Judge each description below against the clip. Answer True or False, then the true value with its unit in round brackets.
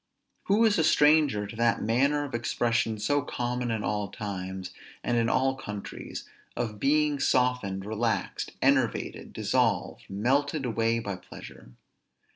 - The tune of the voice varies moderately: True (4.7 semitones)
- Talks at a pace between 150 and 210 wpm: False (135 wpm)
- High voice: False (120 Hz)